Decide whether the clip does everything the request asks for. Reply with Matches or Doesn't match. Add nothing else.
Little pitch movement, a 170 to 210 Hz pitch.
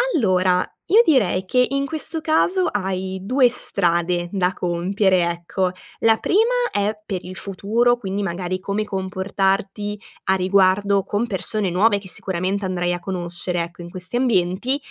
Doesn't match